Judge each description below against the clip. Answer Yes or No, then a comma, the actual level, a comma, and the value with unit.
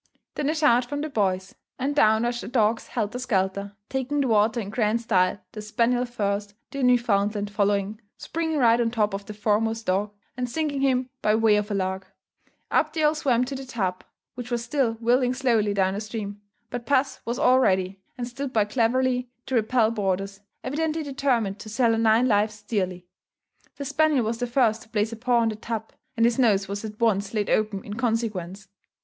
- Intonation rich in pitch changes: No, average, 3.4 semitones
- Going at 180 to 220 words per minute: Yes, average, 200 wpm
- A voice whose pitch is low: No, high, 225 Hz